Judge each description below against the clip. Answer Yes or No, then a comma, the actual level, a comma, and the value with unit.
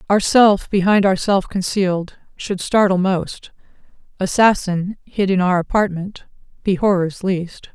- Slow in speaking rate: Yes, slow, 115 wpm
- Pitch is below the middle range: No, high, 190 Hz